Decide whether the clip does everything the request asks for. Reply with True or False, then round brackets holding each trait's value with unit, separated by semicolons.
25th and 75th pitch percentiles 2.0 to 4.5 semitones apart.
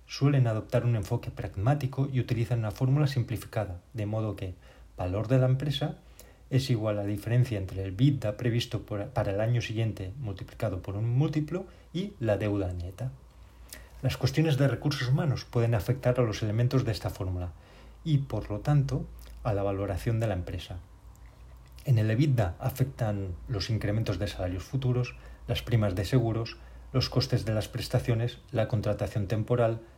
True (3.9 semitones)